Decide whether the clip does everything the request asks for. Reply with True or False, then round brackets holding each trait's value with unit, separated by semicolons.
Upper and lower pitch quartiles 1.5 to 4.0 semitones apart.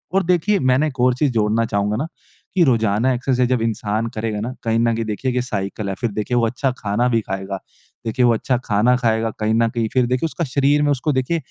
True (2.9 semitones)